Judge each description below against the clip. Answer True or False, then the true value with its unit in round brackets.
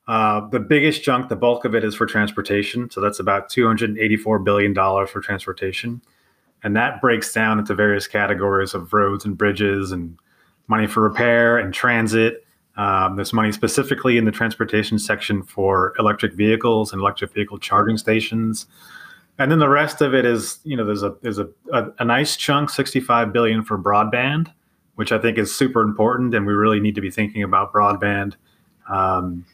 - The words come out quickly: False (180 wpm)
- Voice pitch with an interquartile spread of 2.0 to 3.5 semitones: True (2.6 semitones)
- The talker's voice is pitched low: True (110 Hz)